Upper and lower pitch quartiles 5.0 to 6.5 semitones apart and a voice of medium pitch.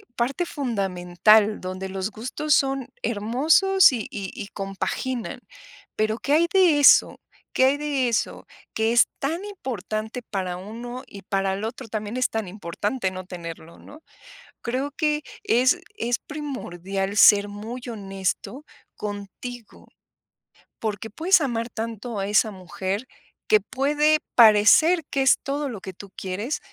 No: wide, 5.4 semitones; high, 225 Hz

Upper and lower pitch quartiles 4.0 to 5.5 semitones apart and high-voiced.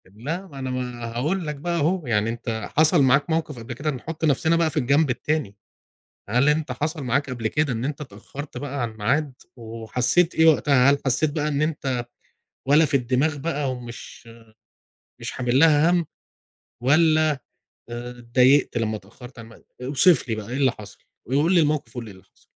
No: average, 4.3 semitones; low, 135 Hz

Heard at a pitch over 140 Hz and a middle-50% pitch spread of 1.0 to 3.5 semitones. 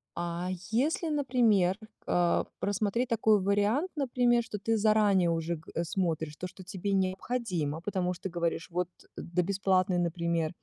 No: high, 190 Hz; average, 4.1 semitones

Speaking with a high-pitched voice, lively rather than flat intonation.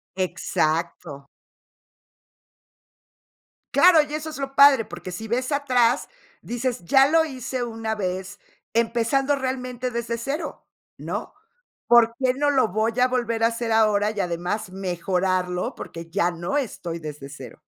Yes: high, 230 Hz; wide, 5.9 semitones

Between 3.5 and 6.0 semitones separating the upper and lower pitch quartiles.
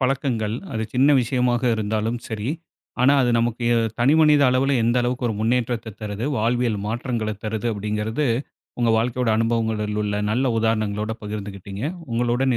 No: narrow, 2.5 semitones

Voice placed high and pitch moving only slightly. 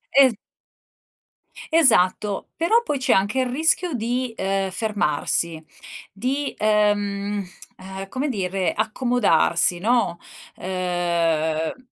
No: high, 205 Hz; wide, 5.6 semitones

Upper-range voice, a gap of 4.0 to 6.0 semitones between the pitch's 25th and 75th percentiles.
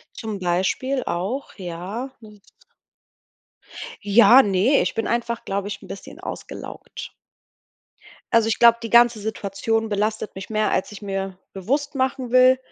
No: high, 220 Hz; average, 3.4 semitones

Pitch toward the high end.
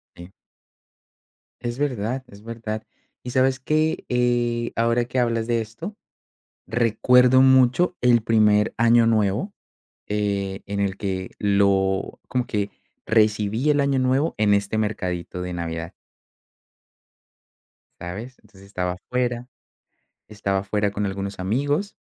No: low, 110 Hz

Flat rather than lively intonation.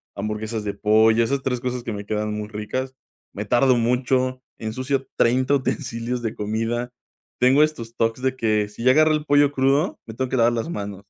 No: average, 3.2 semitones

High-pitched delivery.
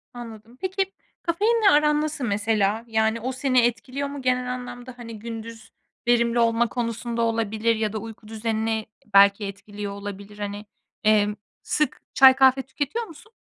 Yes: high, 230 Hz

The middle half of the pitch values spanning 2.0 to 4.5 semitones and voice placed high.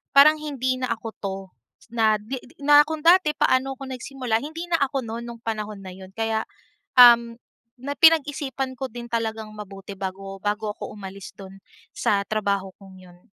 No: average, 5.0 semitones; high, 230 Hz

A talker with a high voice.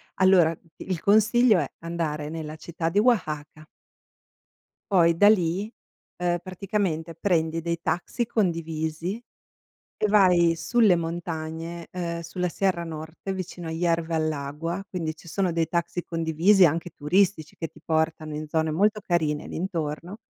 No: medium, 170 Hz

